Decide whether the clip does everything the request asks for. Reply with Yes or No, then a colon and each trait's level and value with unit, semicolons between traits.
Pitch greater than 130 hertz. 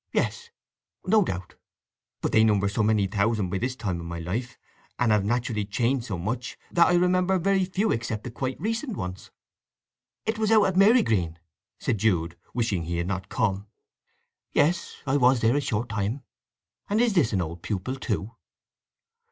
No: low, 115 Hz